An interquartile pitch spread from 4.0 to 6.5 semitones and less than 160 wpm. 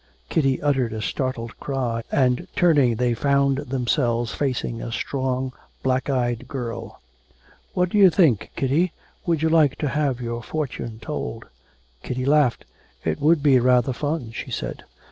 No: average, 3.3 semitones; average, 150 wpm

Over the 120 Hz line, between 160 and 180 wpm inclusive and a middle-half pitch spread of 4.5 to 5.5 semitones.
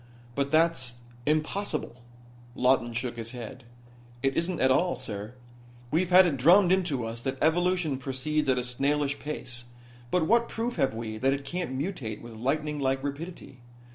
Yes: medium, 140 Hz; average, 165 wpm; average, 5.0 semitones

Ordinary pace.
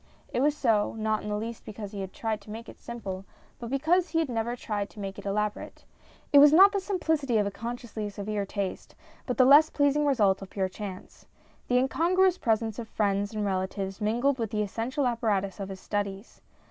No: fast, 210 wpm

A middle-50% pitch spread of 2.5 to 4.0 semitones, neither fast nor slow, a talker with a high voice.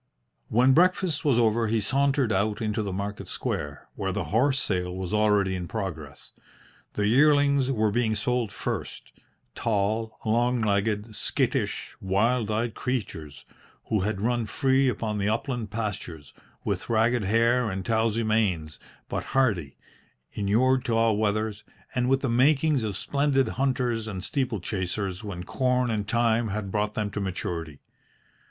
No: average, 3.6 semitones; average, 145 wpm; low, 110 Hz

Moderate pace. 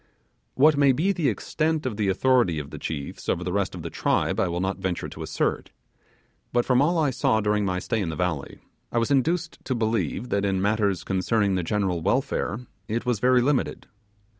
No: fast, 210 wpm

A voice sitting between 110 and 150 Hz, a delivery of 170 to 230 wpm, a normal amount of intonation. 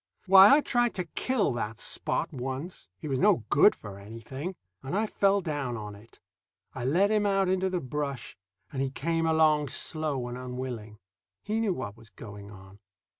No: medium, 140 Hz; average, 180 wpm; wide, 8.0 semitones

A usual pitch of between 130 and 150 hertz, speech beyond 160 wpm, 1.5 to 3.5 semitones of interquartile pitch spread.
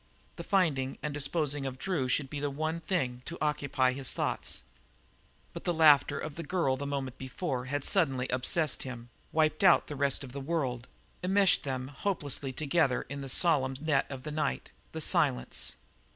Yes: medium, 140 Hz; average, 180 wpm; average, 3.2 semitones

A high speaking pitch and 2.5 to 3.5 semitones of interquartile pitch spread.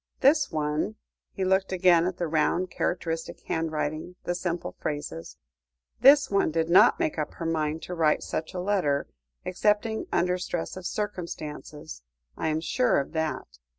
No: medium, 170 Hz; average, 3.1 semitones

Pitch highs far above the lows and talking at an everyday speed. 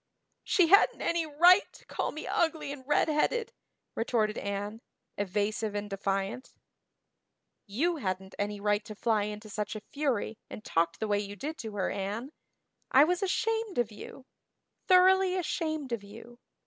Yes: wide, 7.5 semitones; average, 155 wpm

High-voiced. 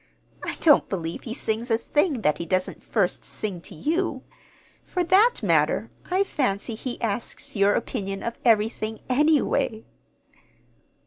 Yes: high, 230 Hz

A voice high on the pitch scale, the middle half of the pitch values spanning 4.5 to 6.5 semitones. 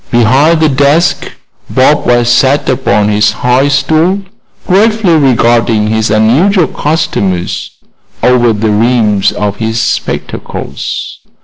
No: low, 125 Hz; wide, 5.5 semitones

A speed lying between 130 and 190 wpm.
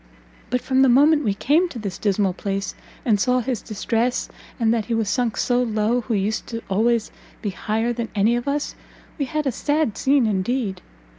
No: average, 200 wpm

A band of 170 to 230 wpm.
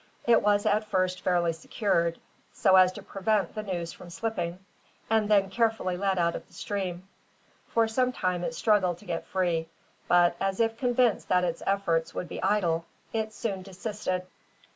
Yes: average, 175 wpm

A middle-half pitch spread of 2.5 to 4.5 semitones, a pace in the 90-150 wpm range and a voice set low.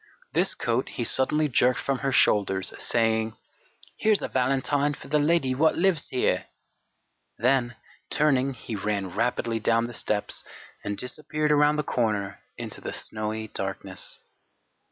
No: average, 4.9 semitones; average, 140 wpm; low, 125 Hz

